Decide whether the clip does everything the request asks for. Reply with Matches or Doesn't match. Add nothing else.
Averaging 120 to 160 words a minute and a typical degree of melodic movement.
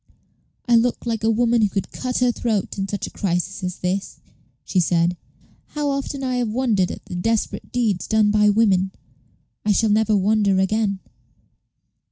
Doesn't match